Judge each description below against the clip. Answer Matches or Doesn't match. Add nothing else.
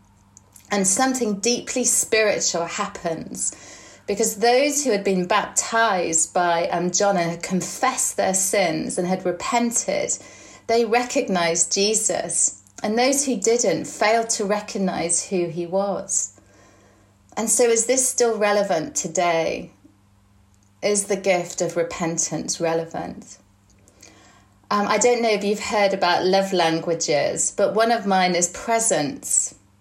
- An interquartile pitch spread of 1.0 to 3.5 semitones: Doesn't match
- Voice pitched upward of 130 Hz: Matches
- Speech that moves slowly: Matches